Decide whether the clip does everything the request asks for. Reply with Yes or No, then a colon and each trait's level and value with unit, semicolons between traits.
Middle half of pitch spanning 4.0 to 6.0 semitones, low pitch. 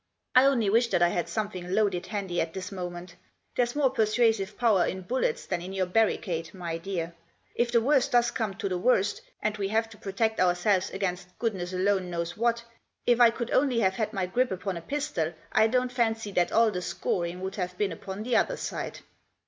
No: average, 4.3 semitones; high, 200 Hz